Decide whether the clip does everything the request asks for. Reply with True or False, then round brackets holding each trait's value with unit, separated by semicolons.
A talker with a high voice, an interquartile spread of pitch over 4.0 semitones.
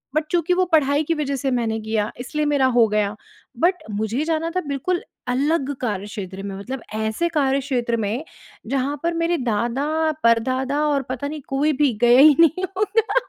True (275 Hz; 5.1 semitones)